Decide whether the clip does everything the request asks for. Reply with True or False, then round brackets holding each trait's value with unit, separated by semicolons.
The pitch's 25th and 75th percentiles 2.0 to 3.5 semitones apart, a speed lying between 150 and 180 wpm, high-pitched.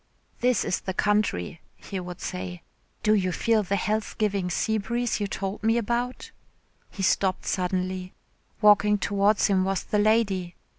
True (2.5 semitones; 155 wpm; 200 Hz)